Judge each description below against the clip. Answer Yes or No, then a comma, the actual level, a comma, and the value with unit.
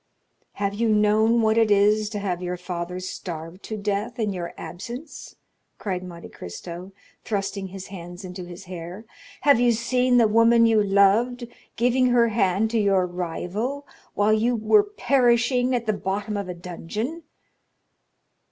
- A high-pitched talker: Yes, high, 210 Hz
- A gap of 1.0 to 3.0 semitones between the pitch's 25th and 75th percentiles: No, average, 4.3 semitones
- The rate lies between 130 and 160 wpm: Yes, average, 155 wpm